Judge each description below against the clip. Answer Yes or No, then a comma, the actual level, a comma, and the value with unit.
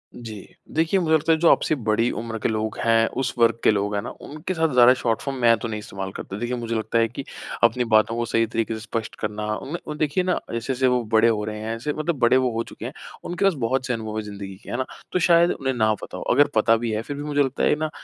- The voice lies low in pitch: Yes, low, 115 Hz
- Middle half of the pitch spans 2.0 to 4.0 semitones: No, average, 4.6 semitones